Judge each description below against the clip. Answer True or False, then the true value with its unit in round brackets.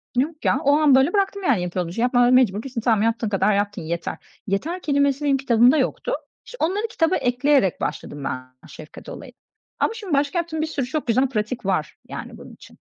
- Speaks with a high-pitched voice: True (260 Hz)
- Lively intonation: True (6.7 semitones)